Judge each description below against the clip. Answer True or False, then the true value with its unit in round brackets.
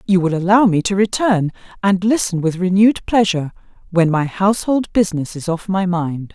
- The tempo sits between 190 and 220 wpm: False (180 wpm)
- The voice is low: False (185 Hz)